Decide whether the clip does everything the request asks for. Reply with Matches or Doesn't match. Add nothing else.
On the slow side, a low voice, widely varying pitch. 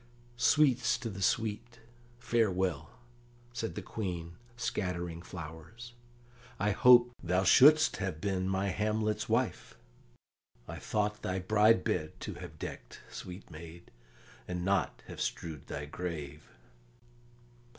Doesn't match